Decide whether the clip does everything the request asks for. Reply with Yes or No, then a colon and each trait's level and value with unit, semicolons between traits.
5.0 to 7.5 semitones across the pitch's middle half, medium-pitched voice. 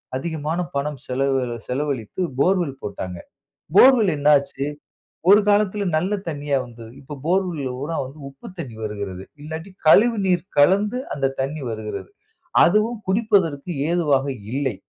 Yes: wide, 5.6 semitones; medium, 145 Hz